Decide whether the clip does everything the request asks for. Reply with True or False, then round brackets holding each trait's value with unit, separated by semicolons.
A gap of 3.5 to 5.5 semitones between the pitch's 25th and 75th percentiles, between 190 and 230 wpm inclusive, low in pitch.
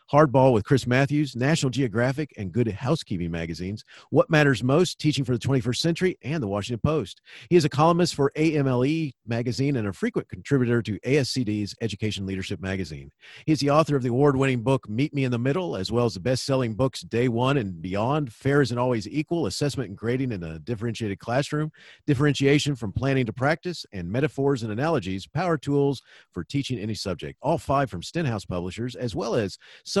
True (4.7 semitones; 195 wpm; 130 Hz)